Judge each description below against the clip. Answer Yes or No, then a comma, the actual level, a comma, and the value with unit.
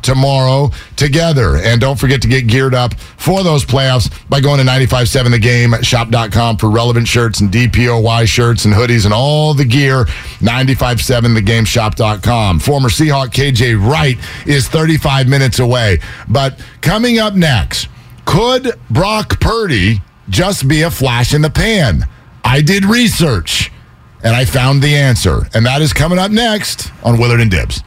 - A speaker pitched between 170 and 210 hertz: No, low, 125 Hz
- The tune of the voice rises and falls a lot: No, average, 3.8 semitones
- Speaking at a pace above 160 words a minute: No, average, 150 wpm